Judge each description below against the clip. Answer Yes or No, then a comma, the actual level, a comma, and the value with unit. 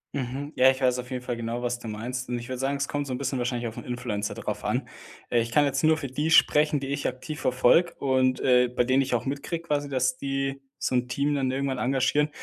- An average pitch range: No, narrow, 2.1 semitones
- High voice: No, low, 130 Hz